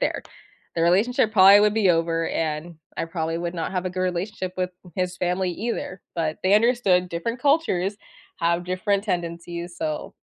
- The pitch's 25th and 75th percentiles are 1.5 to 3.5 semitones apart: Yes, average, 2.9 semitones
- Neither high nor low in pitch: Yes, medium, 180 Hz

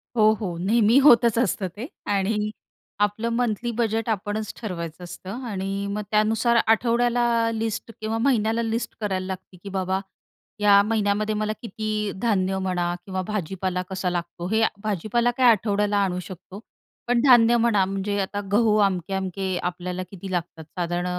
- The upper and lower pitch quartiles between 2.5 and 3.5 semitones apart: Yes, average, 3.1 semitones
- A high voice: Yes, high, 205 Hz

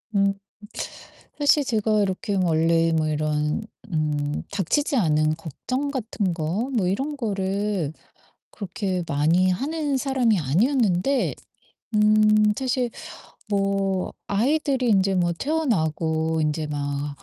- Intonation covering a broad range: Yes, wide, 6.8 semitones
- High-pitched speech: Yes, high, 195 Hz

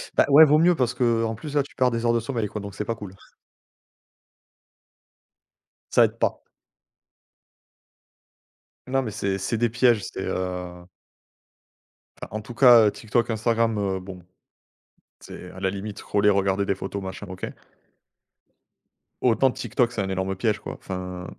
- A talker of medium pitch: No, low, 105 Hz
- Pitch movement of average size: Yes, average, 3.7 semitones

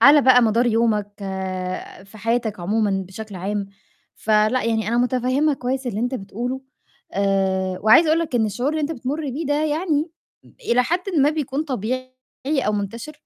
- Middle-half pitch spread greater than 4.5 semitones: Yes, average, 5.0 semitones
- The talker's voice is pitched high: Yes, high, 245 Hz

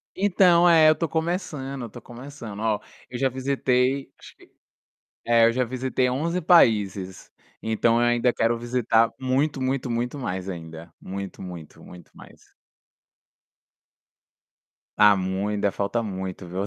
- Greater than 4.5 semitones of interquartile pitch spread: Yes, average, 5.2 semitones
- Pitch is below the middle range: Yes, low, 120 Hz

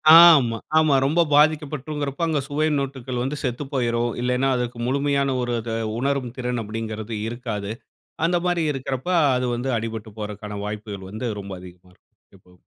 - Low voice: Yes, low, 125 Hz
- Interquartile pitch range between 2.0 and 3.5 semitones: No, average, 4.3 semitones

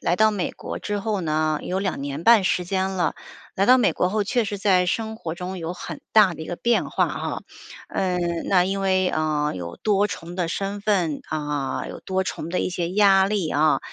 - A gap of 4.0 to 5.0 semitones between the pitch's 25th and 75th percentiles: No, average, 3.5 semitones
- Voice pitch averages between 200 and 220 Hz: No, medium, 185 Hz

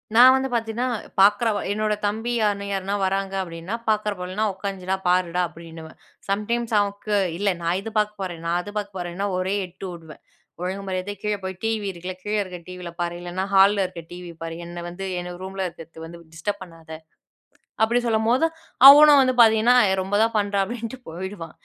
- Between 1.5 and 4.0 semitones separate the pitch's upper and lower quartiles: Yes, average, 3.3 semitones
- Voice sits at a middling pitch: No, high, 195 Hz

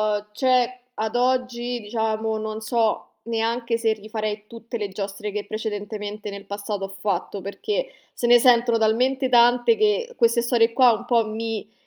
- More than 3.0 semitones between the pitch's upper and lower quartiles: No, narrow, 2.4 semitones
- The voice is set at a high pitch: Yes, high, 225 Hz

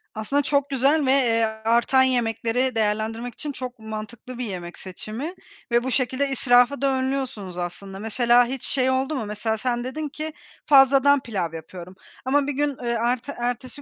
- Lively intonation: No, average, 3.4 semitones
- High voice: Yes, high, 245 Hz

